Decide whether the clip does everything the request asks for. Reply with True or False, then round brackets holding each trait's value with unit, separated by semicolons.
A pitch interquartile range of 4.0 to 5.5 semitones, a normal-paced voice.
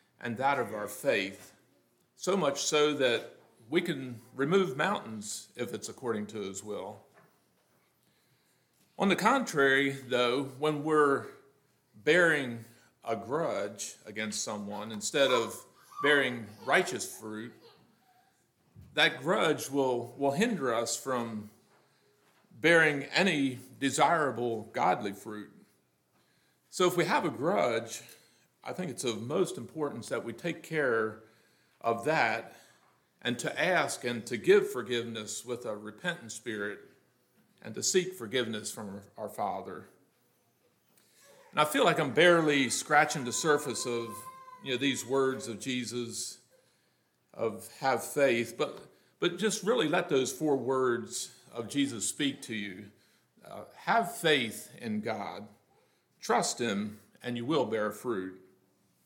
False (5.2 semitones; 130 wpm)